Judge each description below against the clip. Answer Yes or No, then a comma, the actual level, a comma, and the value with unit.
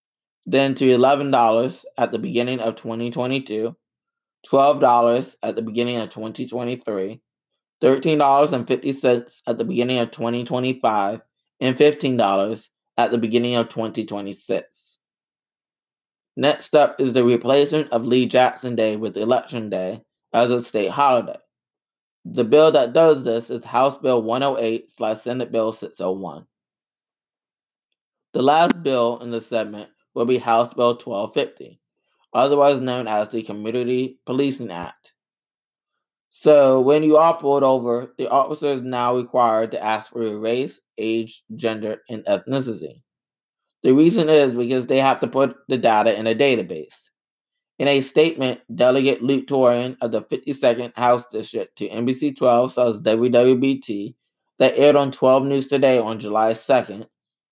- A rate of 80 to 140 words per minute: Yes, slow, 135 wpm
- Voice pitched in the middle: No, low, 120 Hz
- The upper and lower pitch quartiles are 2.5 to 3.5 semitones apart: Yes, average, 2.8 semitones